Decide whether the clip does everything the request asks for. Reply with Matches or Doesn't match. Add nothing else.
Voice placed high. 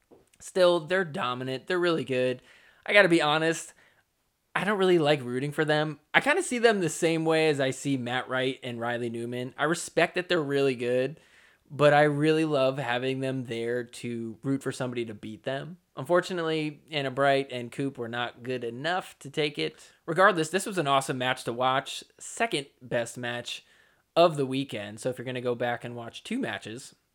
Doesn't match